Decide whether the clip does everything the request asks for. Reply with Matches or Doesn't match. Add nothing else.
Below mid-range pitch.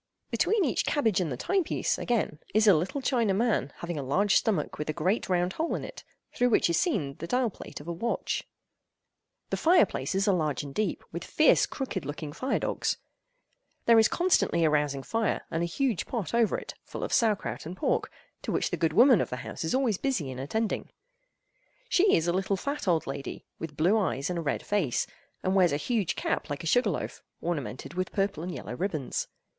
Doesn't match